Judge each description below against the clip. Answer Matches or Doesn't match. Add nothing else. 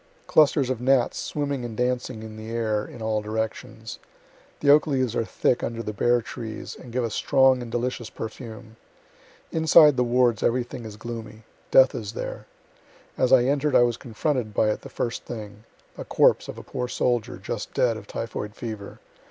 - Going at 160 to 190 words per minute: Matches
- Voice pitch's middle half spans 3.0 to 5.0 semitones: Doesn't match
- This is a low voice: Matches